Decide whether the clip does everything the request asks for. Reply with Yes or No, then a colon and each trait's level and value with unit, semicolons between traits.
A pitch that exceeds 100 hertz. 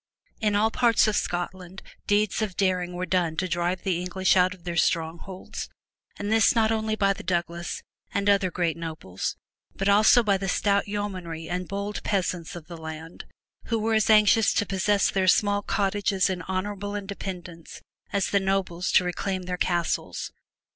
Yes: high, 190 Hz